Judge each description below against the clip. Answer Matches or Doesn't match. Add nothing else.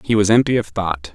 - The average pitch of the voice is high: Doesn't match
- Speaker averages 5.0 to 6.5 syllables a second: Matches